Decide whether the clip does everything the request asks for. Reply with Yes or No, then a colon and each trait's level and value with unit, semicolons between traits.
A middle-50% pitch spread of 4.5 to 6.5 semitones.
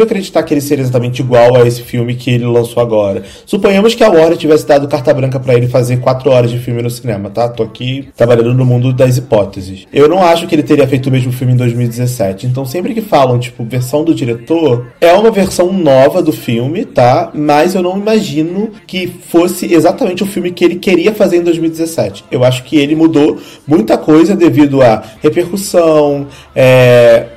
Yes: wide, 5.6 semitones